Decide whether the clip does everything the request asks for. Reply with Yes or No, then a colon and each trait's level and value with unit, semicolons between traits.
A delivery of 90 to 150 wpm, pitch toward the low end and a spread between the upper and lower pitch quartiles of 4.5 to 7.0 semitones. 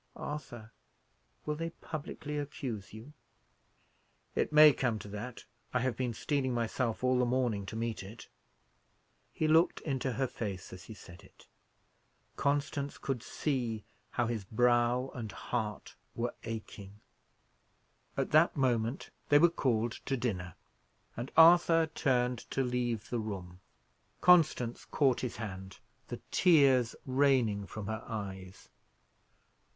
No: slow, 135 wpm; low, 120 Hz; average, 4.1 semitones